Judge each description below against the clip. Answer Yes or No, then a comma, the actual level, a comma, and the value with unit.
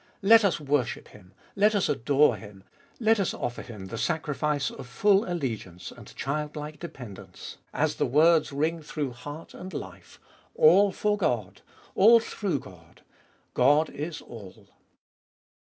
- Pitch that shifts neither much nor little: No, wide, 6.6 semitones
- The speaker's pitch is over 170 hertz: No, medium, 150 Hz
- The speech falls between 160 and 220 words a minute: No, average, 150 wpm